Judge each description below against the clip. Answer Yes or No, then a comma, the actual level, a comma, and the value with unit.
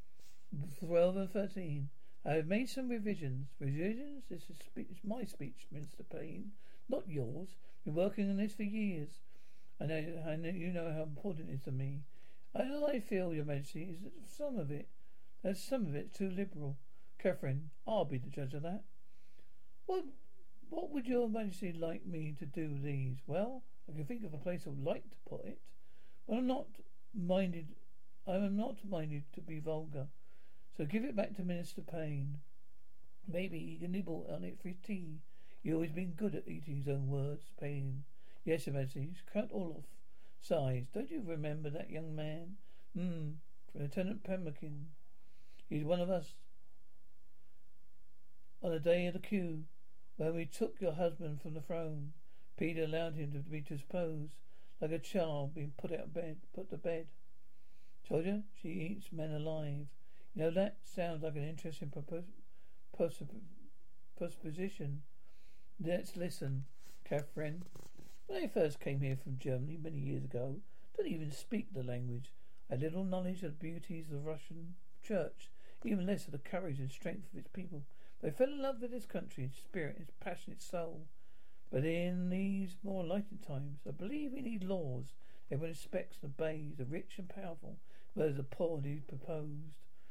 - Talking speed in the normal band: Yes, average, 175 wpm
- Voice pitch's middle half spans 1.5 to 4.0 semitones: No, average, 4.6 semitones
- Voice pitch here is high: No, medium, 165 Hz